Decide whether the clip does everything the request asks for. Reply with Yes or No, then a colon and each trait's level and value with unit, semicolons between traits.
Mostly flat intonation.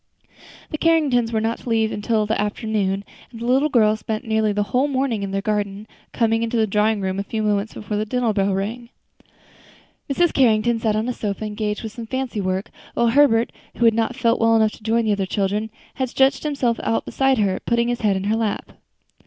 Yes: narrow, 2.3 semitones